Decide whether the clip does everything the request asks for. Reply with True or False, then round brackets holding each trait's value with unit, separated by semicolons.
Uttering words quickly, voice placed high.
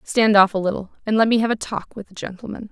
True (285 wpm; 210 Hz)